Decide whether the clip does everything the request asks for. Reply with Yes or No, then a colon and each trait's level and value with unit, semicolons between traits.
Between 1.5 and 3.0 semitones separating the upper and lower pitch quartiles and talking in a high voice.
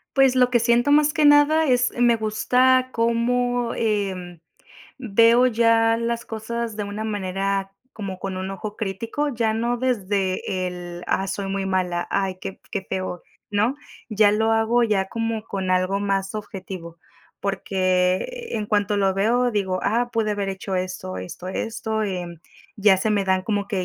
No: average, 3.5 semitones; high, 210 Hz